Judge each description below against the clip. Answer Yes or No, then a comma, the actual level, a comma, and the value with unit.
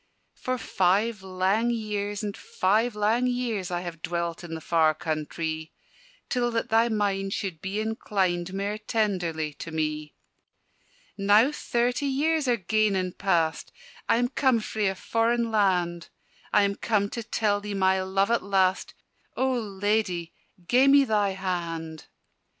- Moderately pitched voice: No, high, 200 Hz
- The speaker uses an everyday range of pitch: Yes, average, 4.2 semitones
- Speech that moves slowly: No, average, 150 wpm